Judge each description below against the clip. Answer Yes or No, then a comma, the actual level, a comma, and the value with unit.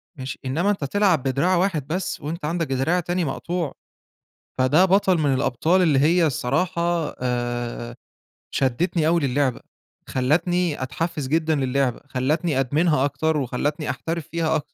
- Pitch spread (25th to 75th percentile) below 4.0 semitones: No, average, 4.4 semitones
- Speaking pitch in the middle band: Yes, medium, 155 Hz